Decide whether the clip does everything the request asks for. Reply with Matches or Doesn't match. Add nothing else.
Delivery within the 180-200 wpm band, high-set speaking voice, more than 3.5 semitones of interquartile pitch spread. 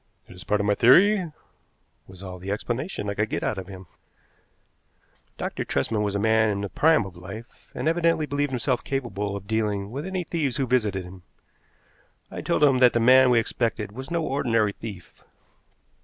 Doesn't match